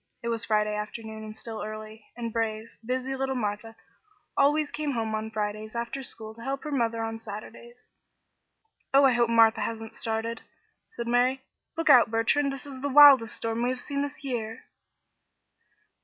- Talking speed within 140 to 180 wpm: Yes, average, 170 wpm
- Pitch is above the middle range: Yes, high, 230 Hz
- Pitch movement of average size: Yes, average, 3.0 semitones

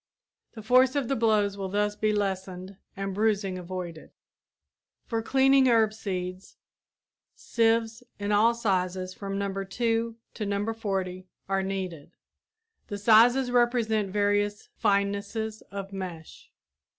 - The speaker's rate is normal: No, slow, 125 wpm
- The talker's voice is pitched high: Yes, high, 205 Hz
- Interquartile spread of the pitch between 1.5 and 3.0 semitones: Yes, average, 2.7 semitones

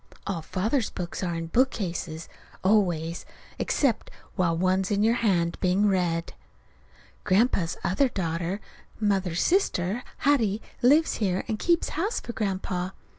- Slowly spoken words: Yes, slow, 125 wpm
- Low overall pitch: No, high, 190 Hz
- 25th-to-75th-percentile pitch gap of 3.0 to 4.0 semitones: No, average, 4.5 semitones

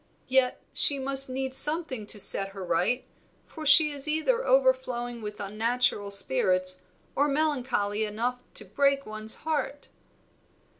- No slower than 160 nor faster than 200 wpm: No, slow, 135 wpm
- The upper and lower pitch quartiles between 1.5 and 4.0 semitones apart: No, wide, 5.5 semitones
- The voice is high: Yes, very high, 255 Hz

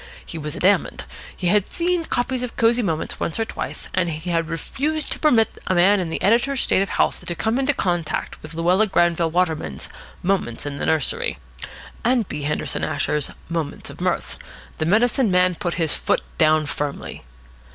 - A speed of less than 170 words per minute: No, average, 180 wpm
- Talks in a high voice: No, medium, 180 Hz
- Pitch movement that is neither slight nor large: No, wide, 6.0 semitones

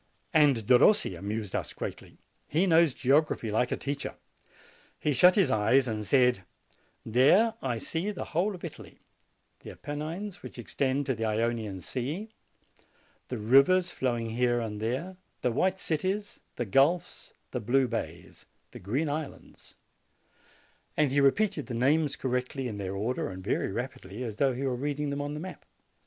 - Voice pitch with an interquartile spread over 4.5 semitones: Yes, average, 4.9 semitones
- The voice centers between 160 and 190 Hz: No, low, 135 Hz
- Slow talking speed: No, average, 165 wpm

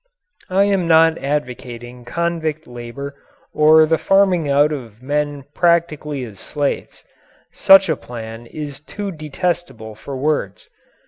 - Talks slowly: Yes, slow, 125 wpm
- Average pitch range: Yes, average, 4.8 semitones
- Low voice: No, medium, 150 Hz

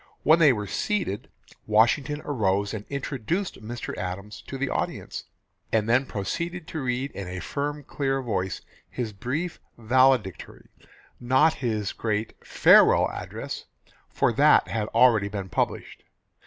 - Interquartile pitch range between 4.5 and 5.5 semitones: Yes, average, 5.1 semitones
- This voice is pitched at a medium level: No, low, 120 Hz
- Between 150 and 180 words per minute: No, slow, 135 wpm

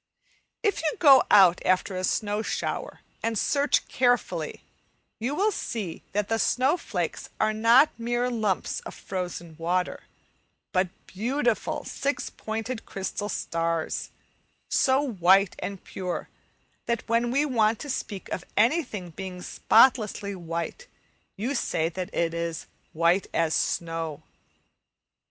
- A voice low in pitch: No, high, 210 Hz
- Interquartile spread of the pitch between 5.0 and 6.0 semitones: Yes, average, 5.3 semitones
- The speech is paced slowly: Yes, slow, 130 wpm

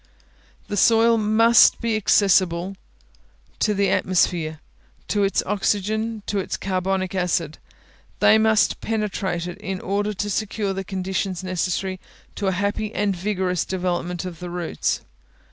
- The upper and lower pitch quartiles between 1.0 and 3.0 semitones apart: Yes, narrow, 2.4 semitones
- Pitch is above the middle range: Yes, high, 195 Hz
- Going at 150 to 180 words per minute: No, slow, 135 wpm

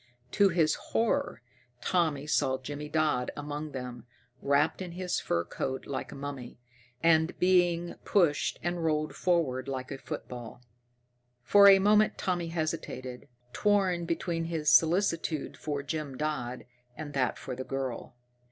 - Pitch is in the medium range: Yes, medium, 155 Hz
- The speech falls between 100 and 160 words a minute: Yes, average, 140 wpm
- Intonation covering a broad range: No, average, 4.4 semitones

